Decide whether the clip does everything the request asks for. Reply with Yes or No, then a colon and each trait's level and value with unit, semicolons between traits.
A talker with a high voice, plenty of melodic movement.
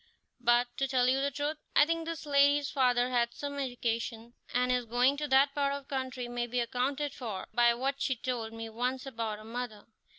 No: very high, 250 Hz; average, 2.7 semitones